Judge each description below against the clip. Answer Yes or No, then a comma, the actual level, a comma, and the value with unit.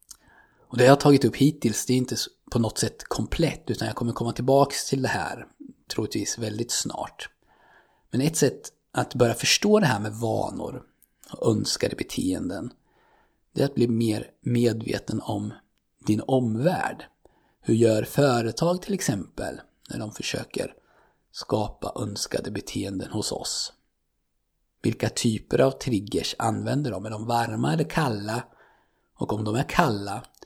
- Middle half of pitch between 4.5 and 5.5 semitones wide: No, average, 4.0 semitones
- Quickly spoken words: No, average, 150 wpm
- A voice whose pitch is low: Yes, low, 120 Hz